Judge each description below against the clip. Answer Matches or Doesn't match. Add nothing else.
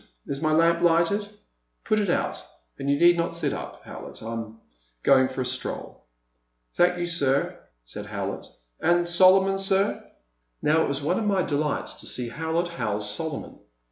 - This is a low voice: Doesn't match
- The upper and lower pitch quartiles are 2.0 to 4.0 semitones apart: Doesn't match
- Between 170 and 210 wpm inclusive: Matches